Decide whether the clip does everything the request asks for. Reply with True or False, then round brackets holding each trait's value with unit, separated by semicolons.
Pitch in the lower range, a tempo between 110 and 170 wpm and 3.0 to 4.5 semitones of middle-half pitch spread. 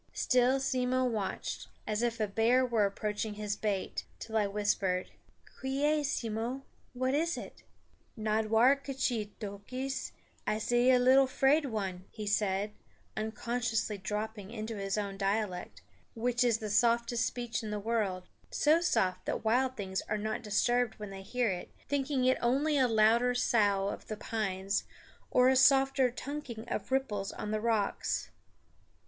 False (225 Hz; 150 wpm; 3.5 semitones)